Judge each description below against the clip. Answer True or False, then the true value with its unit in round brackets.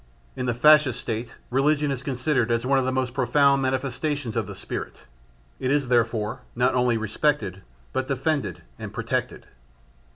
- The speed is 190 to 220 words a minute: False (160 wpm)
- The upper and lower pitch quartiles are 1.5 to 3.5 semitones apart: True (2.7 semitones)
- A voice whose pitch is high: False (130 Hz)